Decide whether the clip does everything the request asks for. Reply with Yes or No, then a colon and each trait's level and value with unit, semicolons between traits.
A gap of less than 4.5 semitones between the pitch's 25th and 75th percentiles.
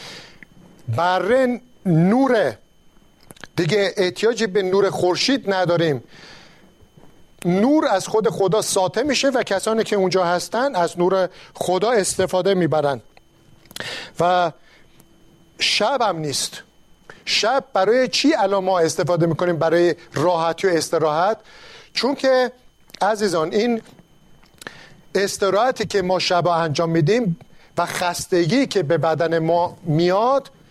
Yes: average, 3.9 semitones